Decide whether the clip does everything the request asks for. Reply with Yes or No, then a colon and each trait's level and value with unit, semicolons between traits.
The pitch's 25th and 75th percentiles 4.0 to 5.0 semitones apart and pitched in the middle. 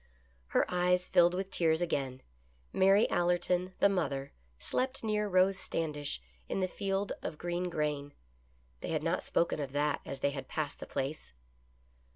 Yes: average, 4.4 semitones; medium, 175 Hz